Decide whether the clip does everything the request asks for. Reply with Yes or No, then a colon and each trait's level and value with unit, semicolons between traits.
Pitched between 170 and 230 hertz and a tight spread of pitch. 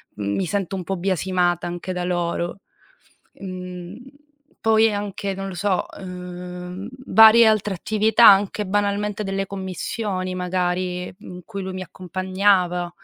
Yes: medium, 185 Hz; narrow, 2.0 semitones